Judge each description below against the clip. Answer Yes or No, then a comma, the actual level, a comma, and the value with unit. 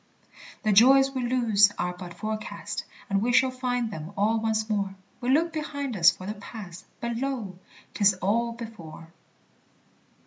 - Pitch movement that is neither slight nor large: Yes, average, 4.1 semitones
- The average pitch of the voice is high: Yes, high, 220 Hz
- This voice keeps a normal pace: Yes, average, 160 wpm